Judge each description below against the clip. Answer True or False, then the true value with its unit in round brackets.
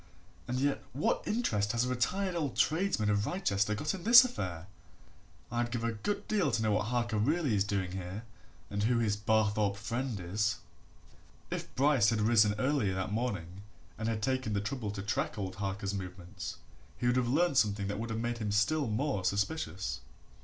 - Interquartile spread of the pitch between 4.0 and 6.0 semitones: True (4.4 semitones)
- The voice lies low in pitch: True (110 Hz)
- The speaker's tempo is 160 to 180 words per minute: False (190 wpm)